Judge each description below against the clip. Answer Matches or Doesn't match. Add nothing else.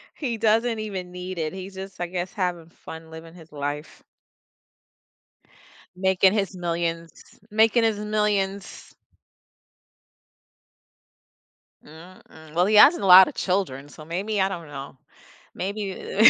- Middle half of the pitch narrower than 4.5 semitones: Matches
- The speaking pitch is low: Doesn't match